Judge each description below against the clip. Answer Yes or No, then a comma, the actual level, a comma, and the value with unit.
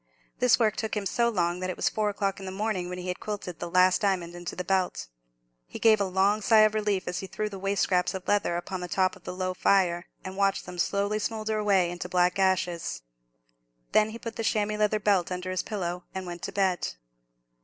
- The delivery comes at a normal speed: No, fast, 235 wpm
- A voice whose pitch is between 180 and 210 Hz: Yes, high, 190 Hz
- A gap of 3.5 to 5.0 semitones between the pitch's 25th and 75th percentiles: No, average, 2.7 semitones